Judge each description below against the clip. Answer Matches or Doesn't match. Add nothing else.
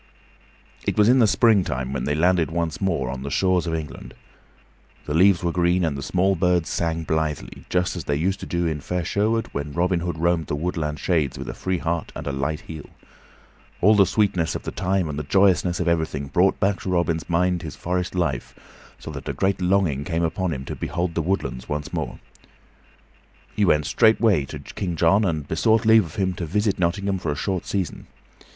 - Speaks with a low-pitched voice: Matches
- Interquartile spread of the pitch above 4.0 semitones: Doesn't match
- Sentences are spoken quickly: Matches